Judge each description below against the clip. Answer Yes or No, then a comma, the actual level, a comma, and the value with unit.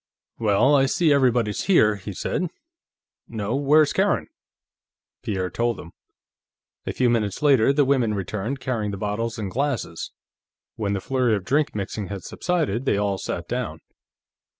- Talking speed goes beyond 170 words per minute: No, average, 150 wpm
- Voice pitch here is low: Yes, low, 115 Hz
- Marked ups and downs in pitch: No, average, 4.9 semitones